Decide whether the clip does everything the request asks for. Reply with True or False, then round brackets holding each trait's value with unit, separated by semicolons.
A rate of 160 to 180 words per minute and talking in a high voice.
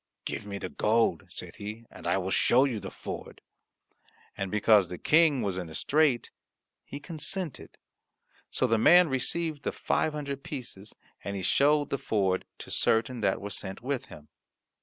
False (175 wpm; 115 Hz)